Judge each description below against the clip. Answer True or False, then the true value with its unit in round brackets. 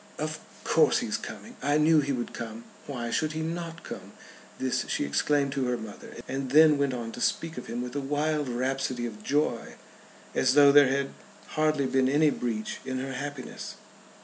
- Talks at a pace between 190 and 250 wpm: True (195 wpm)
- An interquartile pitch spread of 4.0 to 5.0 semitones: False (3.1 semitones)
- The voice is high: False (135 Hz)